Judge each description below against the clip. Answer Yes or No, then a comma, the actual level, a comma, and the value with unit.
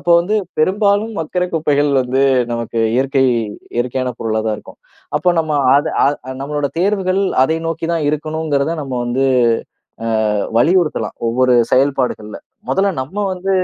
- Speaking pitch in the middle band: Yes, medium, 150 Hz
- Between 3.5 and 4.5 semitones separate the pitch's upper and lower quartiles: No, average, 5.0 semitones